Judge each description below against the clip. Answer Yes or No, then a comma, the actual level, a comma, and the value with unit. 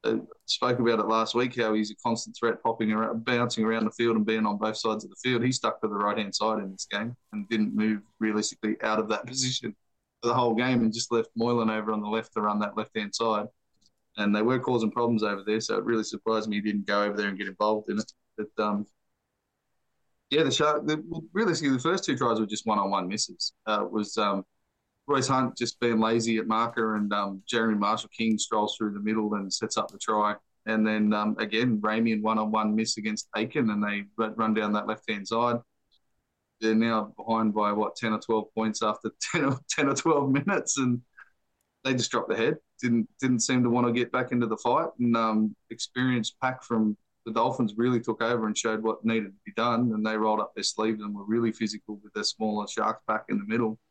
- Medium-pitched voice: No, low, 110 Hz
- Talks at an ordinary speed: No, fast, 230 wpm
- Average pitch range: No, narrow, 1.9 semitones